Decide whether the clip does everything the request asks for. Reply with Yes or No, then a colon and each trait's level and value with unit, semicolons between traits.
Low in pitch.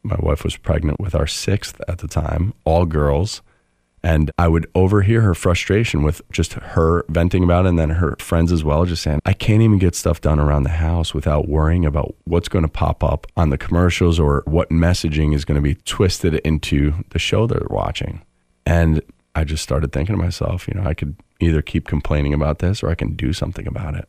Yes: very low, 80 Hz